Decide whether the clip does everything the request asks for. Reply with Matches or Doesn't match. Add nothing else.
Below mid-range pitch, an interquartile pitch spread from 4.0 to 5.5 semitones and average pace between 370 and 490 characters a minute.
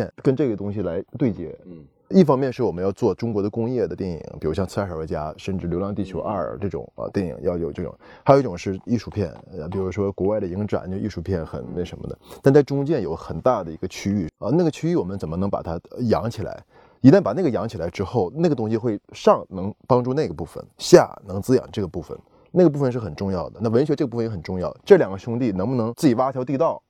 Matches